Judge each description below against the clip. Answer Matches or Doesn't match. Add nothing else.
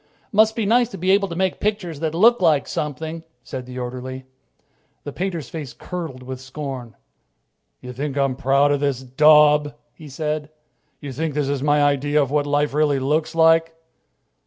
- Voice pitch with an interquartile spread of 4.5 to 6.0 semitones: Doesn't match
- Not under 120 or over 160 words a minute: Doesn't match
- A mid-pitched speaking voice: Matches